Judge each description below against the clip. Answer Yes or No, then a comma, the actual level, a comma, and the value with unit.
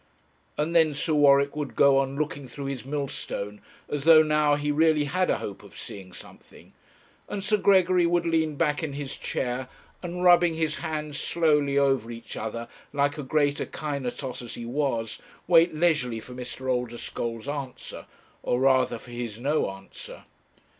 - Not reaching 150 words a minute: No, average, 165 wpm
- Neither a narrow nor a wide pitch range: Yes, average, 3.7 semitones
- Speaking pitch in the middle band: Yes, medium, 145 Hz